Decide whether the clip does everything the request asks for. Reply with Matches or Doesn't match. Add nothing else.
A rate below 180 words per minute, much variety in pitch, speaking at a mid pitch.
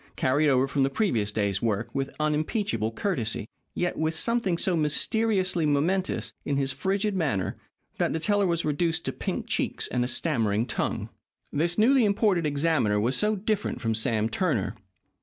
Matches